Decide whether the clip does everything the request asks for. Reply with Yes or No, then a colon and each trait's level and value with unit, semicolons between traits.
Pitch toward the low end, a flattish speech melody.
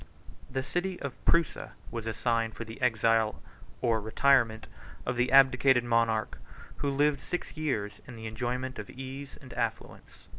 No: low, 125 Hz; average, 3.3 semitones